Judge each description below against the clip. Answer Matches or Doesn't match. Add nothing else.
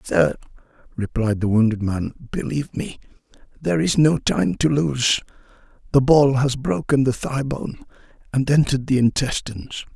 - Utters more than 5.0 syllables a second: Doesn't match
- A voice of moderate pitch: Doesn't match